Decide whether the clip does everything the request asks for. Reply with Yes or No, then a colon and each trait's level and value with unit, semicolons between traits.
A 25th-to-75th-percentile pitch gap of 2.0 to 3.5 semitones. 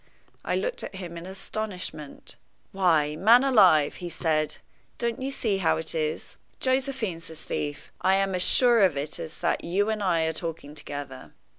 No: wide, 5.4 semitones